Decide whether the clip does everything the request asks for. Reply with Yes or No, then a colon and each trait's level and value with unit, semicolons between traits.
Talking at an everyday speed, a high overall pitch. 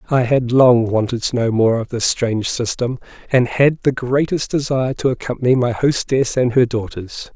No: average, 190 wpm; low, 125 Hz